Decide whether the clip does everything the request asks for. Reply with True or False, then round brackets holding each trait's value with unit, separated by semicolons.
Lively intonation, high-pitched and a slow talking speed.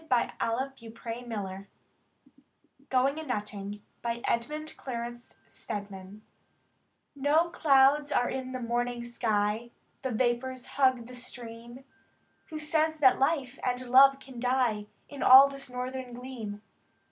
False (2.6 semitones; 250 Hz; 125 wpm)